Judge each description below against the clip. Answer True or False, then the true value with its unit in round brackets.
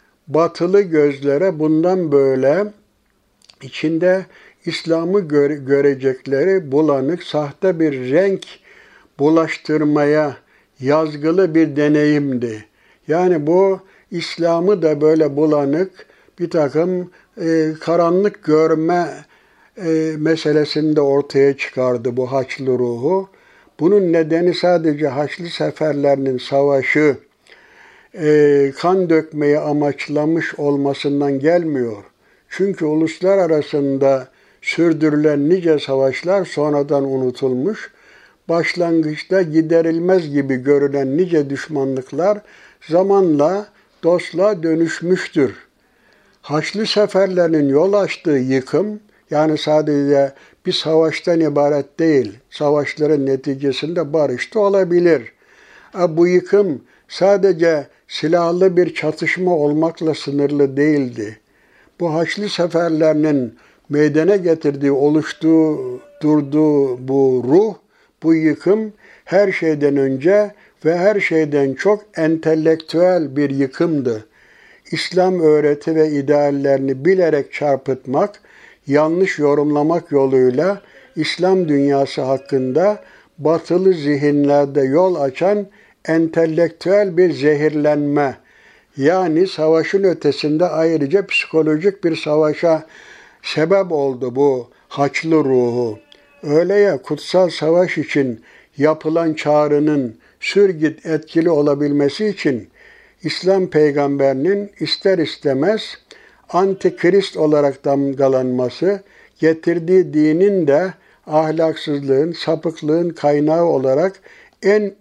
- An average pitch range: True (3.7 semitones)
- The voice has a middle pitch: True (155 Hz)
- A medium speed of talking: False (85 wpm)